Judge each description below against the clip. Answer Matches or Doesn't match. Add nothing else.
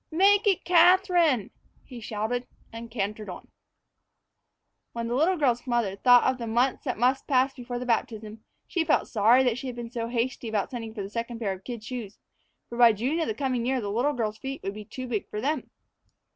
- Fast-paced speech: Matches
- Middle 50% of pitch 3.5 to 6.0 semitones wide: Doesn't match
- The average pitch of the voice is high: Matches